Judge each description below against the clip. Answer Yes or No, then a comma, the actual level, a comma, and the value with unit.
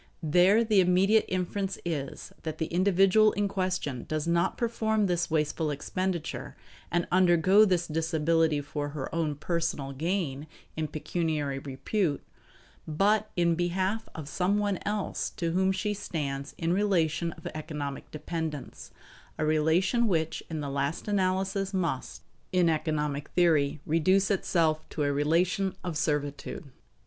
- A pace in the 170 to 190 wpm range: No, average, 140 wpm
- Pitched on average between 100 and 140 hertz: No, medium, 170 Hz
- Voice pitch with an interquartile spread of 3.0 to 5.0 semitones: Yes, average, 3.8 semitones